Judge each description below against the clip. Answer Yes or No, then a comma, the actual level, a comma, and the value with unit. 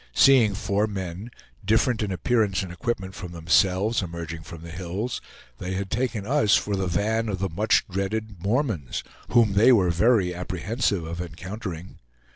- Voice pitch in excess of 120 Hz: No, very low, 95 Hz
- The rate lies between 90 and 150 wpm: No, average, 160 wpm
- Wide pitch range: No, average, 3.9 semitones